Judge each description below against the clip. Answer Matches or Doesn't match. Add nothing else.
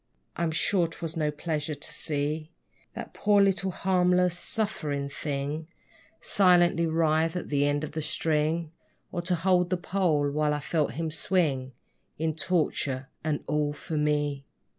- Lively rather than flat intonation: Doesn't match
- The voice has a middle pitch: Matches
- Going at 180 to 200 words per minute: Doesn't match